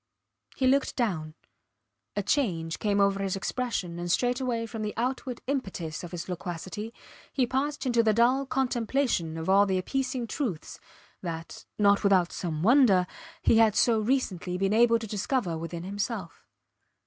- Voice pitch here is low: No, high, 210 Hz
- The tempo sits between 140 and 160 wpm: Yes, average, 155 wpm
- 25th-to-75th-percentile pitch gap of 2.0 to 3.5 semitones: No, wide, 5.6 semitones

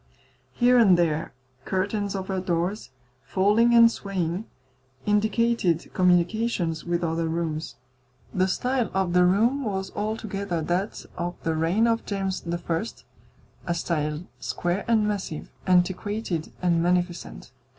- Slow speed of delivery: Yes, slow, 120 wpm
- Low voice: No, medium, 185 Hz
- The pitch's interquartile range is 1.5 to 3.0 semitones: No, average, 3.5 semitones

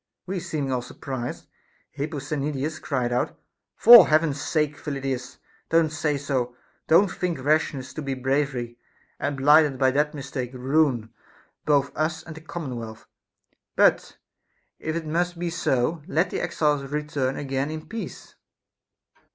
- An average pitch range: Yes, average, 3.1 semitones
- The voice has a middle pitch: Yes, medium, 145 Hz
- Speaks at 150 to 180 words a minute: No, average, 140 wpm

